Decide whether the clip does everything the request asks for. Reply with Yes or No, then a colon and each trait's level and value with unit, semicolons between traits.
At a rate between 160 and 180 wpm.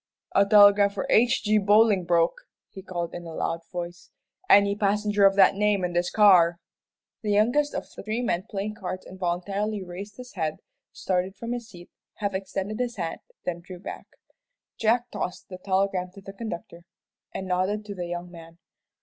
Yes: average, 175 wpm